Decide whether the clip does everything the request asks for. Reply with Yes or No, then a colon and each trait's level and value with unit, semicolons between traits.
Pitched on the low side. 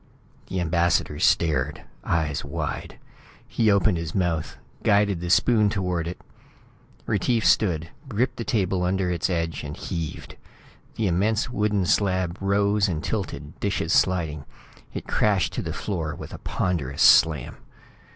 Yes: very low, 90 Hz